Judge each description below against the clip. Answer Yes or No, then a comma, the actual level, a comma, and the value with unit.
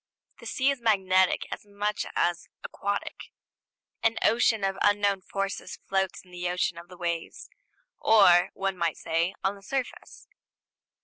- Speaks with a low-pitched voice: No, high, 195 Hz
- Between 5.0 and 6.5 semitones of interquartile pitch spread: No, narrow, 2.6 semitones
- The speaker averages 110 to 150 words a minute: Yes, average, 145 wpm